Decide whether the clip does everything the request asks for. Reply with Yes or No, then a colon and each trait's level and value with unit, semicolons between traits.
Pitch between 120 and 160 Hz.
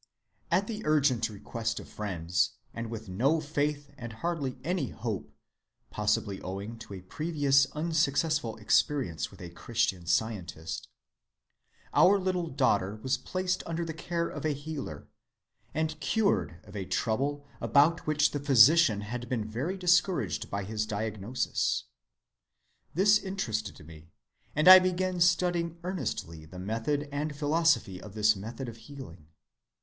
Yes: low, 135 Hz